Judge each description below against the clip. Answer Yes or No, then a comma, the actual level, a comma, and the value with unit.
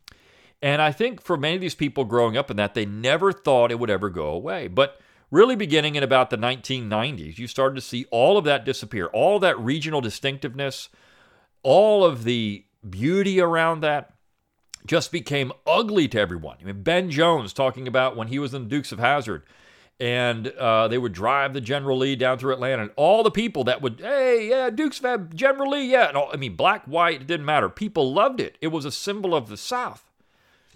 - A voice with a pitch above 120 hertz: Yes, medium, 140 Hz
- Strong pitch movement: Yes, wide, 5.8 semitones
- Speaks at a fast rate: Yes, fast, 210 wpm